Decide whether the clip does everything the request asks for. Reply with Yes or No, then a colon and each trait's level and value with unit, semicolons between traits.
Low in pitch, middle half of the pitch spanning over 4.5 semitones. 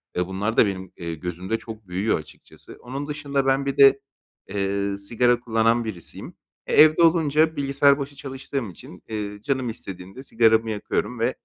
Yes: low, 115 Hz; wide, 5.6 semitones